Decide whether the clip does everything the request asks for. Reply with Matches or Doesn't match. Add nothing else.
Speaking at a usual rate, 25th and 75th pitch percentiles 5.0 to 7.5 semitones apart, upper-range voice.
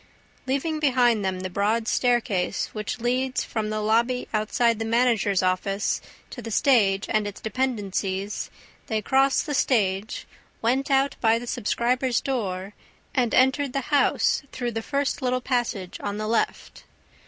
Doesn't match